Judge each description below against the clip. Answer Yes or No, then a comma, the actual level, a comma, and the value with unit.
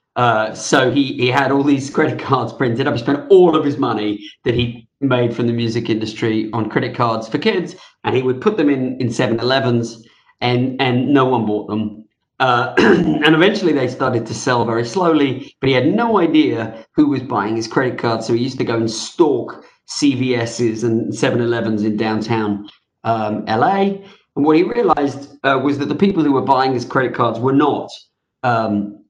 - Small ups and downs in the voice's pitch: No, average, 3.8 semitones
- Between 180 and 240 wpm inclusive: Yes, average, 195 wpm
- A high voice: No, low, 125 Hz